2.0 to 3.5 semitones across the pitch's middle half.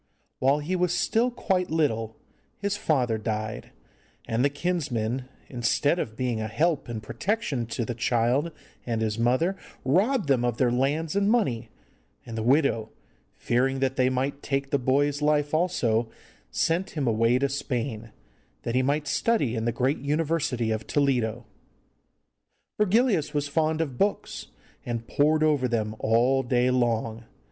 No: average, 4.8 semitones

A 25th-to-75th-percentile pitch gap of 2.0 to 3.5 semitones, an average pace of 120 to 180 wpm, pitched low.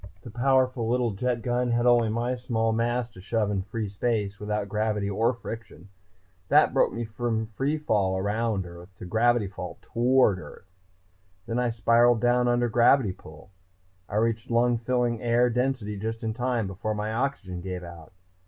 Yes: average, 2.9 semitones; average, 170 wpm; low, 115 Hz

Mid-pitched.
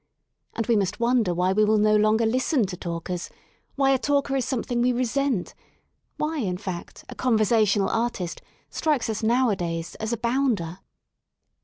No: high, 225 Hz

